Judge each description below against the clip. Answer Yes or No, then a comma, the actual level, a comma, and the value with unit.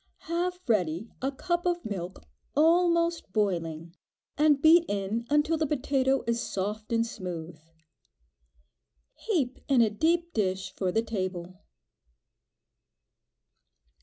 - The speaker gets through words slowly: Yes, slow, 110 wpm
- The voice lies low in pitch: No, high, 235 Hz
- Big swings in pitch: Yes, wide, 9.0 semitones